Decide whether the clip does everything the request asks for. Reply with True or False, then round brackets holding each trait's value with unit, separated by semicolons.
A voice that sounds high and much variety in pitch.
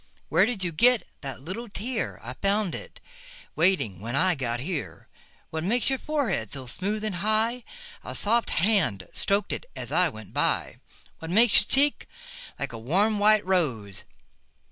True (195 Hz; 7.8 semitones)